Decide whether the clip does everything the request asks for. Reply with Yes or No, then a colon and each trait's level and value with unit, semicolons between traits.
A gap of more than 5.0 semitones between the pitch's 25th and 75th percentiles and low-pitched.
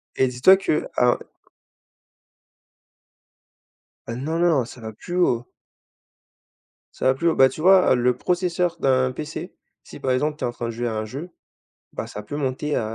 Yes: wide, 5.4 semitones; low, 130 Hz